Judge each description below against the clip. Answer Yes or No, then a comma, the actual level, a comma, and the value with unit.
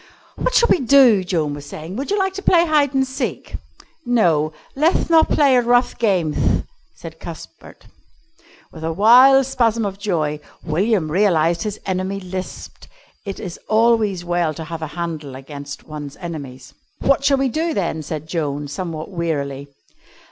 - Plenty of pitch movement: Yes, wide, 7.7 semitones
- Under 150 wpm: No, average, 165 wpm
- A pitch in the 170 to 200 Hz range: Yes, medium, 185 Hz